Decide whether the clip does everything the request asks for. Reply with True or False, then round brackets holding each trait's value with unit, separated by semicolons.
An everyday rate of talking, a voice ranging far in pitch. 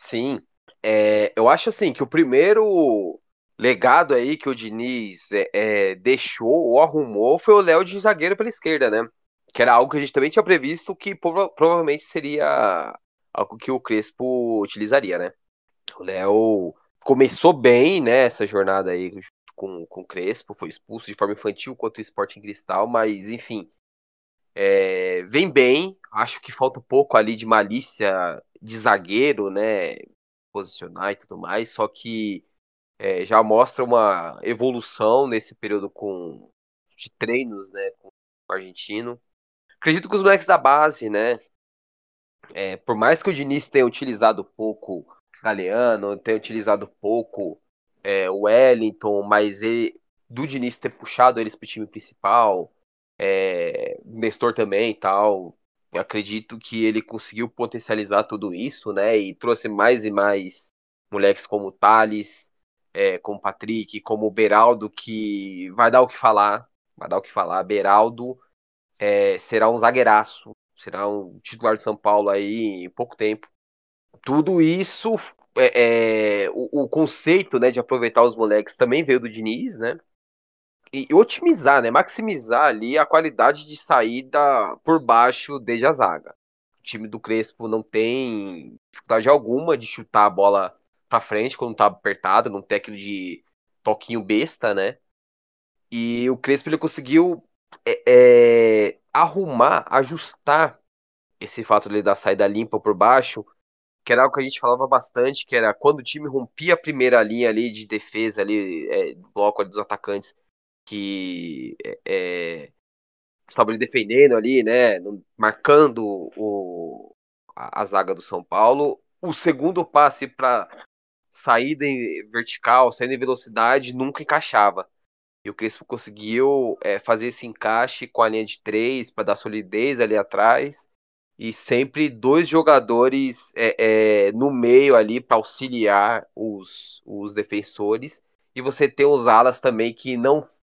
True (150 wpm; 7.0 semitones)